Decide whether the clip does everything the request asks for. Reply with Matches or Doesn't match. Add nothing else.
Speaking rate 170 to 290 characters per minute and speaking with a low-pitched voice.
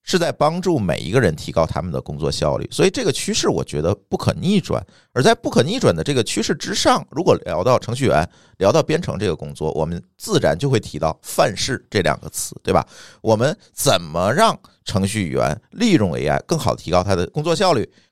Doesn't match